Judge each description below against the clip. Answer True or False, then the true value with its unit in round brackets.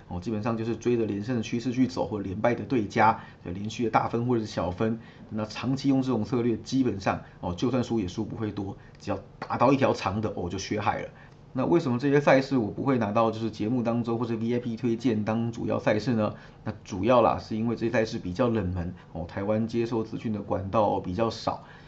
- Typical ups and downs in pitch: False (2.1 semitones)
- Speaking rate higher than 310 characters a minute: True (345 characters per minute)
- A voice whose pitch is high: False (115 Hz)